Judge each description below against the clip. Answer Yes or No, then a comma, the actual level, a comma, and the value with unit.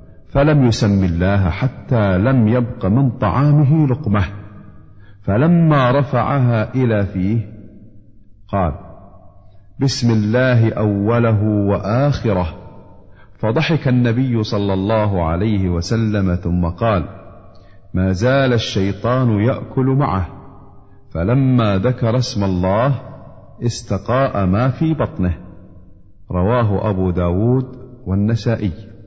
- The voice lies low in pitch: Yes, low, 105 Hz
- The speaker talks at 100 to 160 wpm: No, average, 90 wpm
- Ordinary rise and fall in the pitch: Yes, average, 4.3 semitones